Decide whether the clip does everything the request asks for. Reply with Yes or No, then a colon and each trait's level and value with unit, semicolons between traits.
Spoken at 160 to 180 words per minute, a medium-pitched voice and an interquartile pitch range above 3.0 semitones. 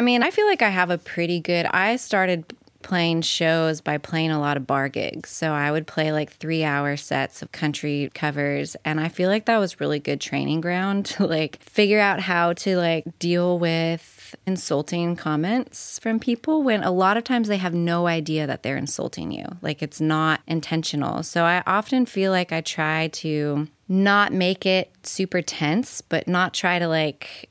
No: average, 195 wpm; medium, 170 Hz; average, 3.5 semitones